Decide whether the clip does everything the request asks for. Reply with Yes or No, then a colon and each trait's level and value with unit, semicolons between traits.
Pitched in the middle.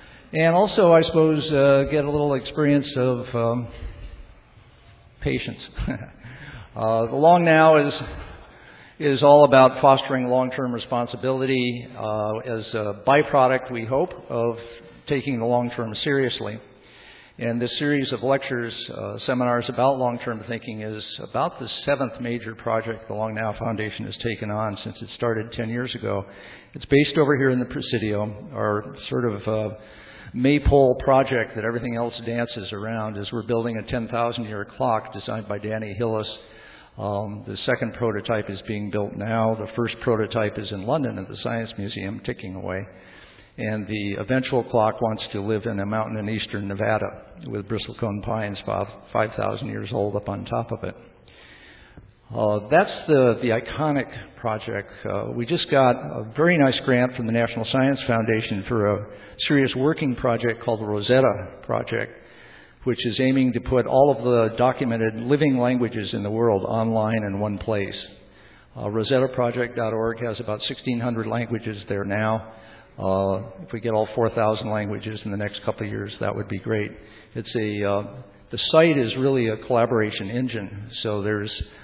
No: low, 115 Hz